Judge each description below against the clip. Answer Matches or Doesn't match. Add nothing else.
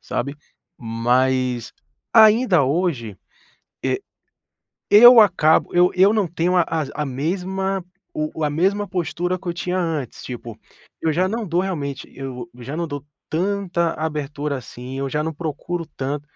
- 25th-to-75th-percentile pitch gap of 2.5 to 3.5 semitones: Doesn't match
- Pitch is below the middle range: Doesn't match